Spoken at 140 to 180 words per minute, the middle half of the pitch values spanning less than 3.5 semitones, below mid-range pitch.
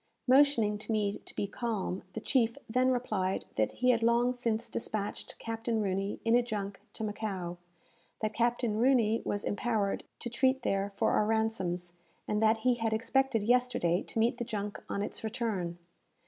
No: average, 175 wpm; average, 2.9 semitones; high, 220 Hz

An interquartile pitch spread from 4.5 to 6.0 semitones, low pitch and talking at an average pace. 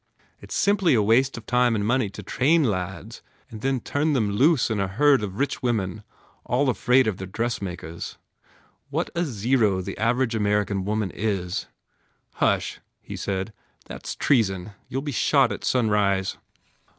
Yes: average, 4.8 semitones; low, 110 Hz; average, 170 wpm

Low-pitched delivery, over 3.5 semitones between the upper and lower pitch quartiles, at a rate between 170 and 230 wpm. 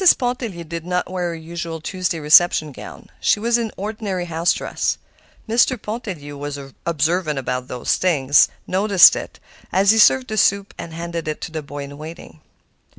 No: medium, 170 Hz; average, 4.6 semitones; average, 175 wpm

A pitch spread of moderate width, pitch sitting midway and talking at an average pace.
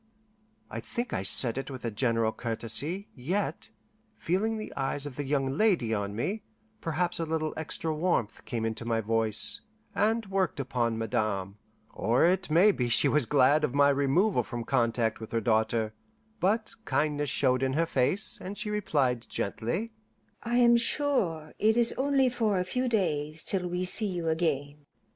No: wide, 8.4 semitones; medium, 150 Hz; average, 170 wpm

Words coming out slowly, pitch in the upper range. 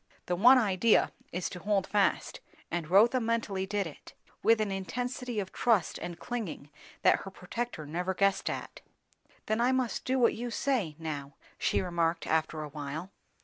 No: average, 170 wpm; high, 195 Hz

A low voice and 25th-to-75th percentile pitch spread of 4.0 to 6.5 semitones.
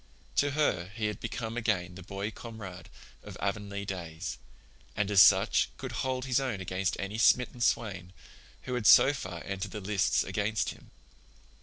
No: low, 100 Hz; average, 3.4 semitones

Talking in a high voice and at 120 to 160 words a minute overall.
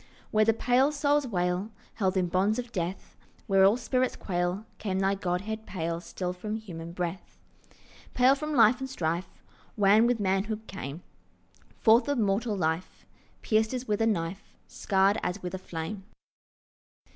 Yes: high, 200 Hz; average, 155 wpm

